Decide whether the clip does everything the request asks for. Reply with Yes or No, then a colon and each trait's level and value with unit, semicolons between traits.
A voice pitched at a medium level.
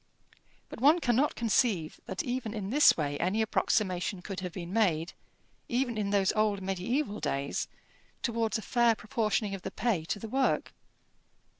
No: high, 215 Hz